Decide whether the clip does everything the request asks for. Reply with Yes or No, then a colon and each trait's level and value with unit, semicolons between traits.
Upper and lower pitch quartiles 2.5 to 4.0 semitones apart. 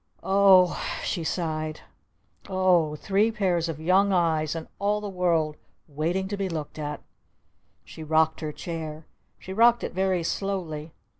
Yes: average, 3.5 semitones